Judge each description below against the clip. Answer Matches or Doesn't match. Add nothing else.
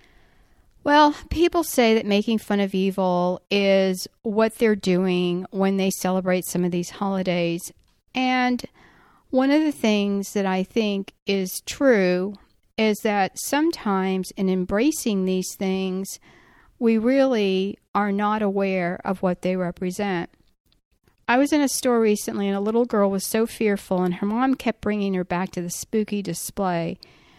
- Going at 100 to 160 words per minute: Matches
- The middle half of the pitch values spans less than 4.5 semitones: Matches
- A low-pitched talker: Doesn't match